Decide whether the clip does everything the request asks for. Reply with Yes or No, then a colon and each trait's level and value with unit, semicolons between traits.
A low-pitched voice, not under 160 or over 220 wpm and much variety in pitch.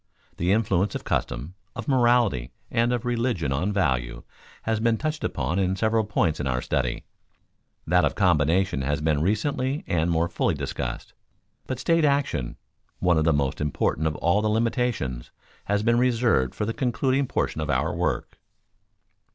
Yes: very low, 95 Hz; average, 165 wpm; wide, 7.8 semitones